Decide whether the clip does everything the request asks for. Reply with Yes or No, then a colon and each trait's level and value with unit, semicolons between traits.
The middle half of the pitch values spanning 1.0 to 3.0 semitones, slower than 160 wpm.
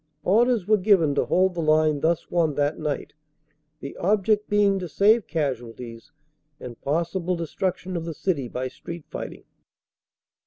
No: average, 4.9 semitones; average, 150 wpm